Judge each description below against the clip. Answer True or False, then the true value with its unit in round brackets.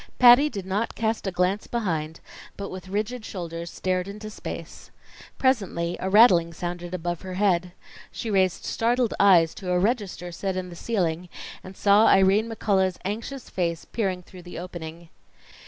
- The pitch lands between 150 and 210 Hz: True (190 Hz)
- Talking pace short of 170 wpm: True (160 wpm)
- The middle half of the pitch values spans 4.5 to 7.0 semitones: False (3.3 semitones)